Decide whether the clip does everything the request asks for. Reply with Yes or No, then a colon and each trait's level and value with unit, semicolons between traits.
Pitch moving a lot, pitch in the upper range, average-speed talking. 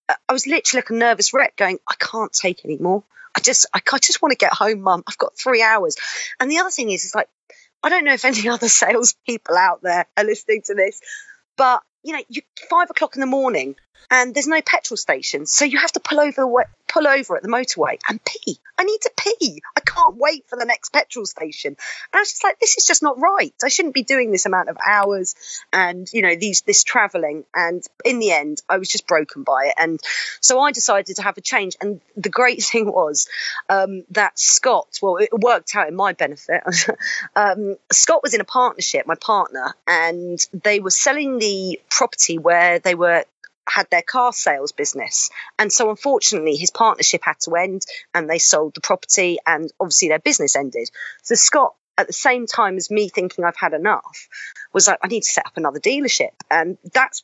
No: wide, 7.3 semitones; high, 230 Hz; fast, 215 wpm